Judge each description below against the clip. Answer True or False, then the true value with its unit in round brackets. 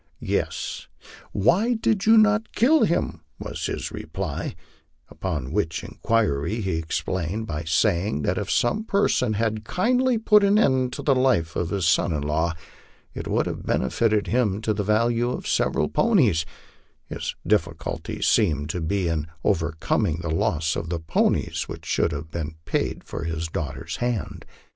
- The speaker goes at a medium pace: True (160 wpm)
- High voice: False (100 Hz)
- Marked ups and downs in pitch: True (7.8 semitones)